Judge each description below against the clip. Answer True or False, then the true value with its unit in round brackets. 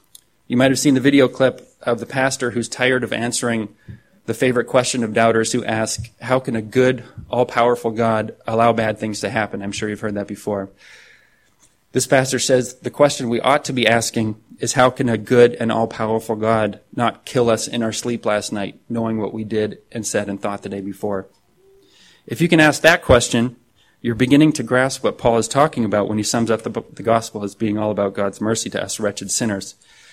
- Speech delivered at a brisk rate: True (215 wpm)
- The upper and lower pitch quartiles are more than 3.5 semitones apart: False (2.8 semitones)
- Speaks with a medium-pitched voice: False (115 Hz)